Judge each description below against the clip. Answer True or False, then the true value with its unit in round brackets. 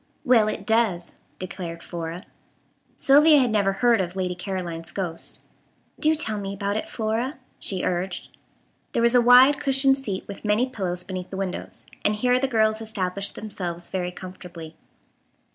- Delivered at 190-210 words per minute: False (160 wpm)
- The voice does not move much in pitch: False (4.6 semitones)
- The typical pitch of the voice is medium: False (200 Hz)